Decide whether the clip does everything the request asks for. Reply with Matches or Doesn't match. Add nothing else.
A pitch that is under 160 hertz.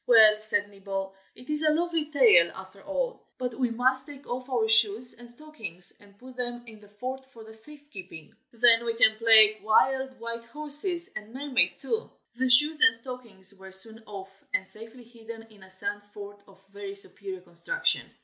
Doesn't match